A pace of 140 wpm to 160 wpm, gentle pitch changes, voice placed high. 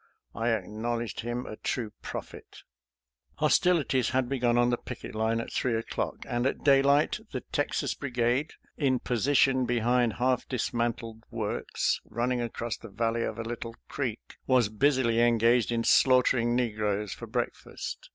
No: average, 145 wpm; narrow, 1.8 semitones; low, 120 Hz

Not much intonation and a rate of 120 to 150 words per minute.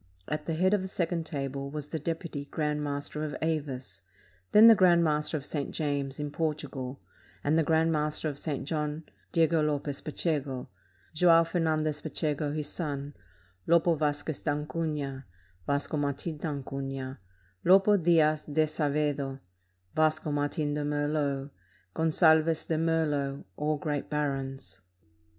Yes: narrow, 2.1 semitones; slow, 135 wpm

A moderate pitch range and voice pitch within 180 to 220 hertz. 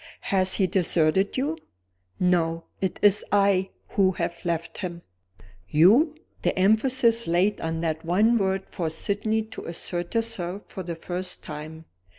Yes: average, 3.6 semitones; medium, 185 Hz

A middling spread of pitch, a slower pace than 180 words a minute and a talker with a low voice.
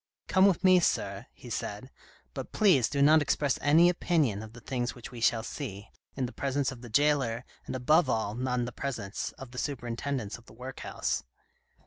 No: average, 3.7 semitones; fast, 205 wpm; low, 130 Hz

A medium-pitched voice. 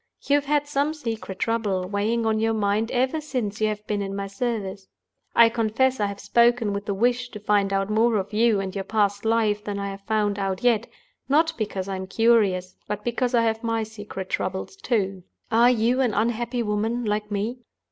No: high, 220 Hz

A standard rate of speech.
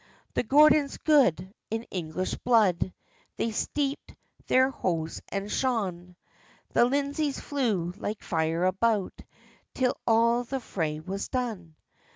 No: slow, 120 wpm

